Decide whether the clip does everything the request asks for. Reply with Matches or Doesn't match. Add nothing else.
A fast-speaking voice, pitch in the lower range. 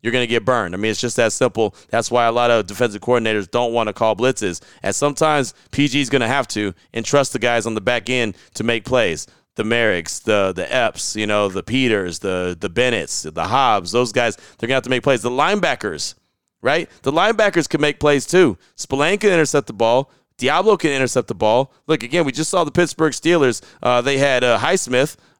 Matches